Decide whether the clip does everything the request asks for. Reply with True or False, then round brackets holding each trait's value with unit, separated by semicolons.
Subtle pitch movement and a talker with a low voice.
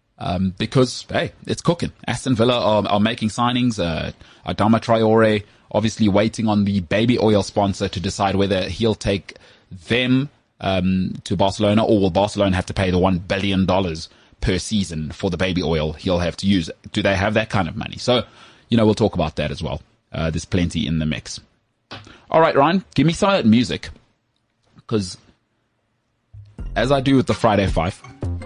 False (3.5 semitones; 105 Hz)